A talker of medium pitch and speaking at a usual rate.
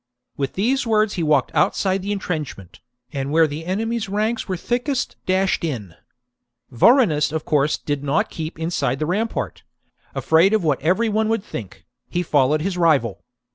Yes: medium, 170 Hz; average, 165 wpm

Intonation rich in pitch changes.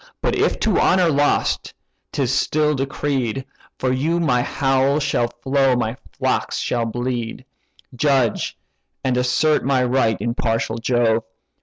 No: average, 2.8 semitones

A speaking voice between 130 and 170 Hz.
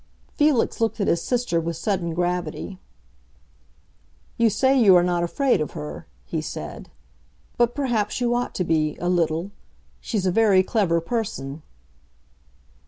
No: medium, 185 Hz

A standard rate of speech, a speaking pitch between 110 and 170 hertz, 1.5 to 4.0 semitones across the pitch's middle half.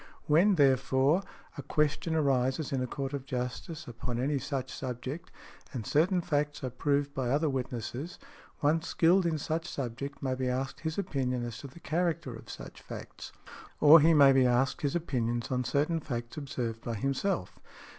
Yes: average, 175 wpm; medium, 140 Hz; average, 3.6 semitones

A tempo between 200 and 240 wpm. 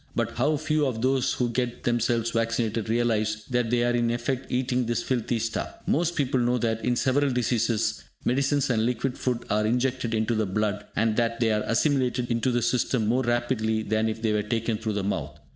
Yes: fast, 205 wpm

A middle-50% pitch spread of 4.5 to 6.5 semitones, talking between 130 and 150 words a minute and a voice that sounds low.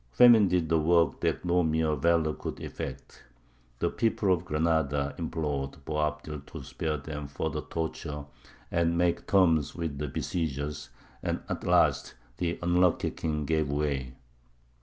No: narrow, 2.5 semitones; average, 140 wpm; very low, 80 Hz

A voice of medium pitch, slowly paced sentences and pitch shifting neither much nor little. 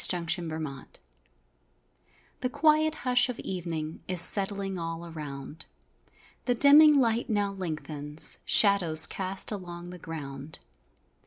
Yes: medium, 180 Hz; slow, 120 wpm; average, 5.0 semitones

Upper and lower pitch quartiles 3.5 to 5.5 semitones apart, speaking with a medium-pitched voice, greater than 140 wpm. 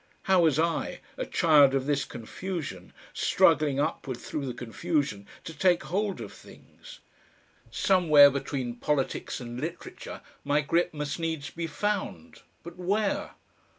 No: average, 4.2 semitones; medium, 150 Hz; slow, 135 wpm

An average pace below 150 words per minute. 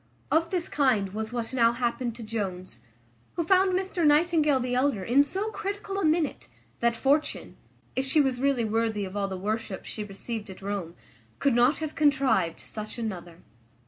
No: average, 175 wpm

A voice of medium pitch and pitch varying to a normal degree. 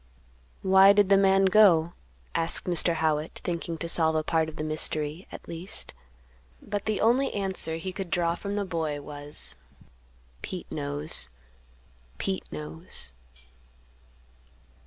Yes: medium, 170 Hz; average, 3.8 semitones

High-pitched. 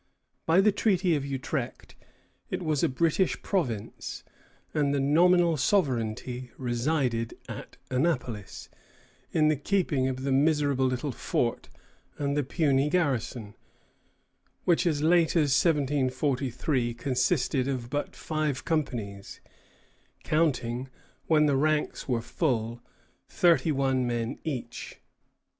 No: medium, 140 Hz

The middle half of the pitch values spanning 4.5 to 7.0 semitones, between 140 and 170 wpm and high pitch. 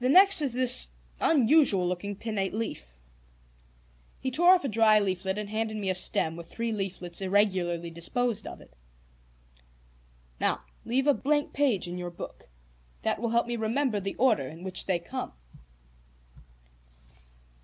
Yes: average, 5.3 semitones; average, 155 wpm; high, 210 Hz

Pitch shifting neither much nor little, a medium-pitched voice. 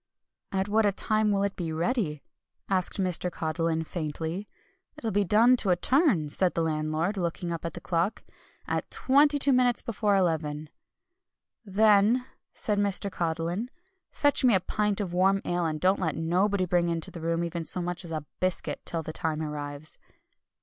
Yes: average, 4.0 semitones; medium, 180 Hz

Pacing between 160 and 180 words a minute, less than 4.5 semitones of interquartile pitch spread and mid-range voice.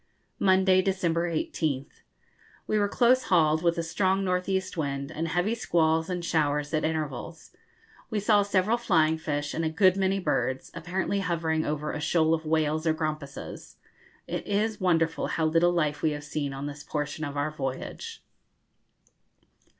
Yes: average, 165 wpm; average, 3.6 semitones; medium, 165 Hz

